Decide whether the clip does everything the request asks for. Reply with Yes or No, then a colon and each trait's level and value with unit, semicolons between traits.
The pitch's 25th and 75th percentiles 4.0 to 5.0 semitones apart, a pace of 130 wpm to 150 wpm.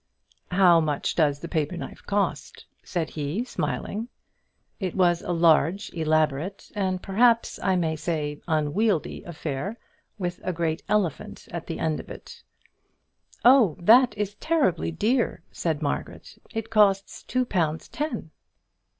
Yes: average, 4.6 semitones; average, 140 wpm